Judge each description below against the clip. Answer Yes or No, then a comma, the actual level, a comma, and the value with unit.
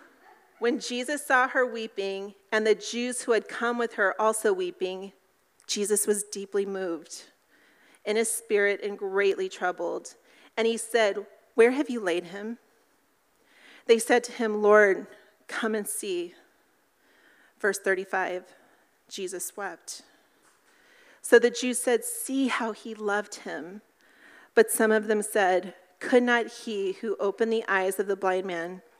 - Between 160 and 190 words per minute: No, average, 145 wpm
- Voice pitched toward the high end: Yes, high, 220 Hz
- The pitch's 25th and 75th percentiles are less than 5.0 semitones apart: Yes, average, 3.3 semitones